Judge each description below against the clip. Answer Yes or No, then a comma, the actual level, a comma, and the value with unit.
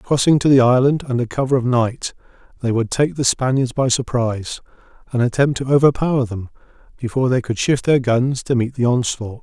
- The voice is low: Yes, low, 125 Hz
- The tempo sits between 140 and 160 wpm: No, average, 190 wpm